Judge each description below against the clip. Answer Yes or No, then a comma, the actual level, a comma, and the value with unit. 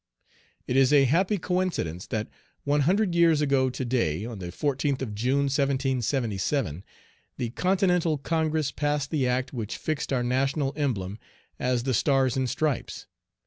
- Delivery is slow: No, average, 150 wpm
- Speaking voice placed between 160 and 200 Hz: No, low, 135 Hz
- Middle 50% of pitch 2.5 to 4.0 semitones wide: Yes, average, 3.5 semitones